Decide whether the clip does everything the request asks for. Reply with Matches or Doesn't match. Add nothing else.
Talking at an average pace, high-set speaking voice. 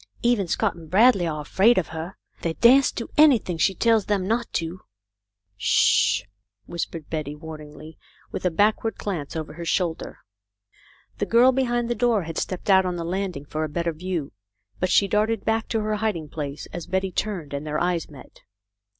Doesn't match